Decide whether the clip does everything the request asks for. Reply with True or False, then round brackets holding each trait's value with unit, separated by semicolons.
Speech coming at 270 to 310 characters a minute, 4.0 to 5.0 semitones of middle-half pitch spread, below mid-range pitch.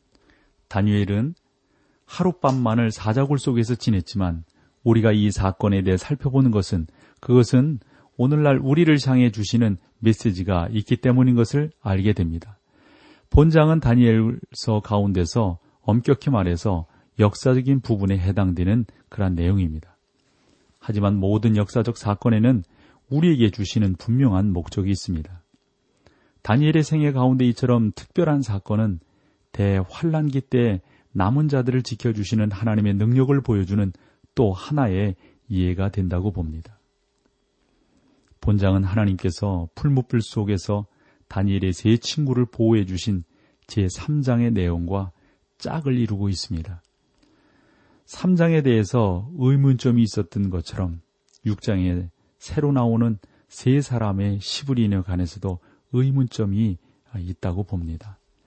True (280 characters per minute; 4.7 semitones; 110 Hz)